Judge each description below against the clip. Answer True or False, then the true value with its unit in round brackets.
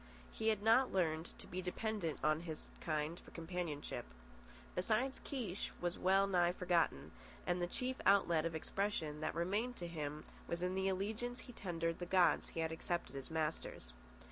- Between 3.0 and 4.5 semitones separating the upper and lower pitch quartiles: True (3.5 semitones)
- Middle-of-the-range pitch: True (175 Hz)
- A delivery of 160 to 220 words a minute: True (170 wpm)